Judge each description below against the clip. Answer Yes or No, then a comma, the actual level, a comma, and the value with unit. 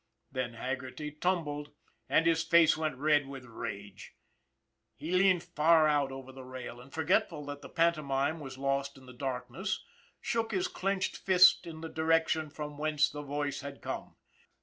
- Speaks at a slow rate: No, average, 165 wpm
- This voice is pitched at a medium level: Yes, medium, 150 Hz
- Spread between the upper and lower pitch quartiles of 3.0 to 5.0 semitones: Yes, average, 3.4 semitones